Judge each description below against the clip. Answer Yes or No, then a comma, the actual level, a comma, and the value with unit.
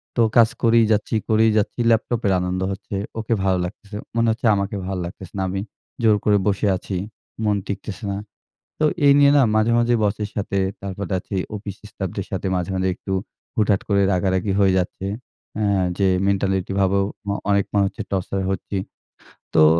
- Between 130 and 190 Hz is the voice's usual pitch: No, low, 100 Hz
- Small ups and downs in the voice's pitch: Yes, narrow, 2.2 semitones